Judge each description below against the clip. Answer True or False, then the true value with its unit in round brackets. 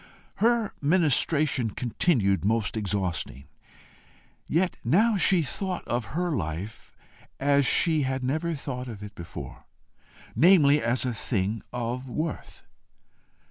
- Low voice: True (130 Hz)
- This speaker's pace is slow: True (115 wpm)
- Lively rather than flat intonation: True (6.8 semitones)